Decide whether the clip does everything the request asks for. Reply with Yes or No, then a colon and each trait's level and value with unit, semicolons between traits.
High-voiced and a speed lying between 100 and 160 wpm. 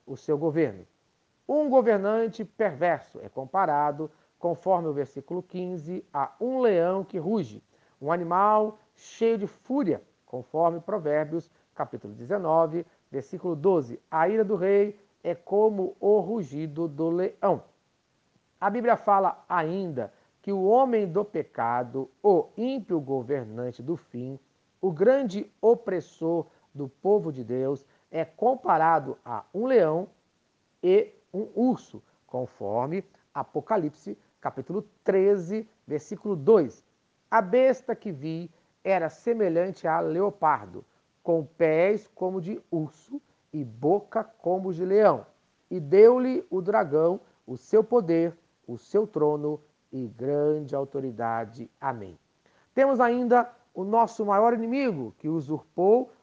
No: medium, 180 Hz; slow, 120 wpm